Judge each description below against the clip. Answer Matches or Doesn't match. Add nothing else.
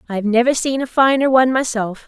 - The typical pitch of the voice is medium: Doesn't match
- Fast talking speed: Matches